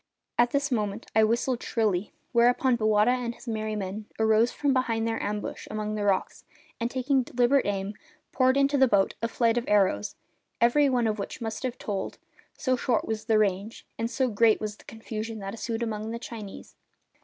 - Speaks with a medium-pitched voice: No, high, 225 Hz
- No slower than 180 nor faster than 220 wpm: Yes, average, 190 wpm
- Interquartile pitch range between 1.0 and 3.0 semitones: Yes, narrow, 2.6 semitones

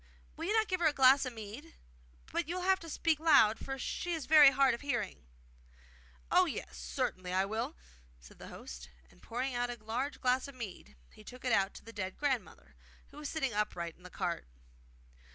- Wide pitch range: Yes, wide, 6.3 semitones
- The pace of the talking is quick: Yes, fast, 210 wpm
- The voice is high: Yes, very high, 250 Hz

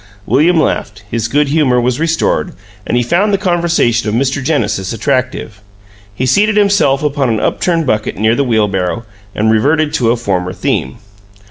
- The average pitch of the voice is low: Yes, low, 130 Hz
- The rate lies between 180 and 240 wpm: No, average, 165 wpm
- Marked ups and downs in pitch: Yes, wide, 6.2 semitones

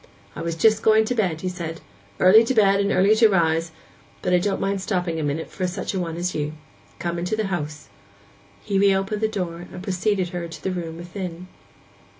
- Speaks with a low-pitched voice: No, medium, 180 Hz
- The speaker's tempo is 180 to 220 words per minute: Yes, fast, 205 wpm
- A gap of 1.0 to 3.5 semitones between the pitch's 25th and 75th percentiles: Yes, average, 2.9 semitones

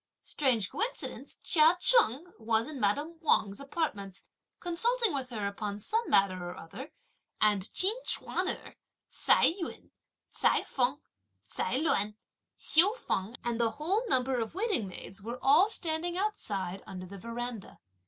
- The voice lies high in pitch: Yes, very high, 255 Hz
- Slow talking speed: No, average, 145 wpm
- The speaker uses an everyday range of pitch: No, wide, 8.7 semitones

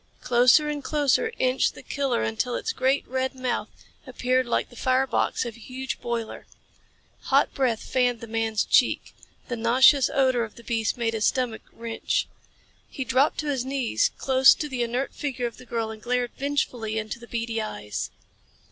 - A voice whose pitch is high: Yes, high, 245 Hz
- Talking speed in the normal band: Yes, average, 180 wpm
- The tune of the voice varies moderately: No, narrow, 2.3 semitones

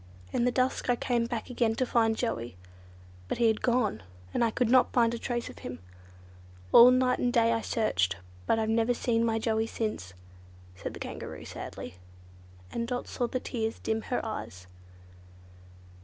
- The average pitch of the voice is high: Yes, high, 230 Hz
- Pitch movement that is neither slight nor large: No, narrow, 1.8 semitones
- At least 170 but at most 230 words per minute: Yes, average, 185 wpm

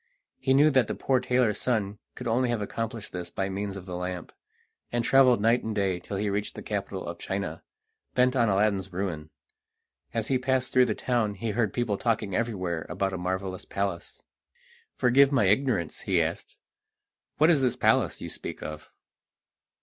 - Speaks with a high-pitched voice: No, low, 105 Hz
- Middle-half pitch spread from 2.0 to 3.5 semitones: No, average, 4.4 semitones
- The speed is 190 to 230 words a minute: No, average, 180 wpm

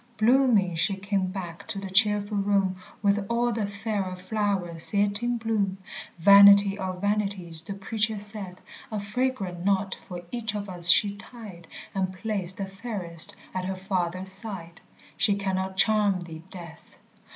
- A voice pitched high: Yes, high, 200 Hz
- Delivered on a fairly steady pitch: Yes, narrow, 2.0 semitones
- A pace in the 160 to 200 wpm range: No, average, 150 wpm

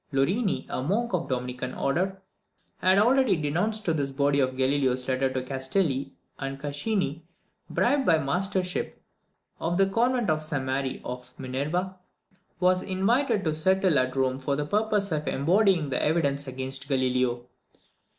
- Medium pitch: Yes, medium, 150 Hz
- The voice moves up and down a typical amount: No, wide, 6.2 semitones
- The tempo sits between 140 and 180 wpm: Yes, average, 150 wpm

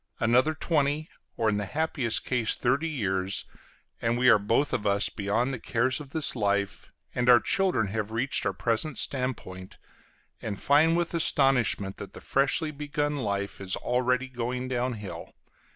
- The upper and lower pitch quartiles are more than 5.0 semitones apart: Yes, wide, 5.4 semitones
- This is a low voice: Yes, low, 125 Hz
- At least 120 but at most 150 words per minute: No, average, 160 wpm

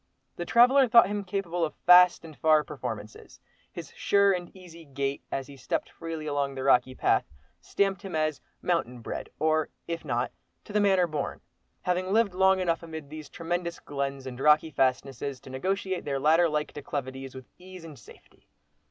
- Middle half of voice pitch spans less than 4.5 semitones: No, average, 4.8 semitones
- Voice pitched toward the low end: No, medium, 160 Hz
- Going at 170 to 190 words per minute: Yes, average, 180 wpm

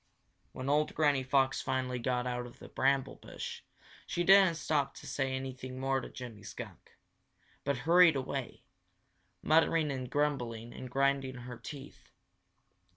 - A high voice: No, low, 135 Hz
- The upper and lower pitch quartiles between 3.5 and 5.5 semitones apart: No, narrow, 2.4 semitones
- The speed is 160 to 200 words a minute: No, average, 145 wpm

